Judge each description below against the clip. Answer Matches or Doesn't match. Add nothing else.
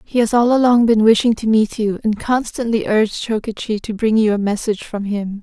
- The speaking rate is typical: Doesn't match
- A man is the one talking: Doesn't match